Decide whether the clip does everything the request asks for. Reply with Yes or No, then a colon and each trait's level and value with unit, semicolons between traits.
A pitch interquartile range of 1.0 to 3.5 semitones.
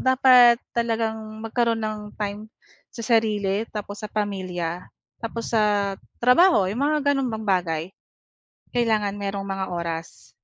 Yes: average, 2.9 semitones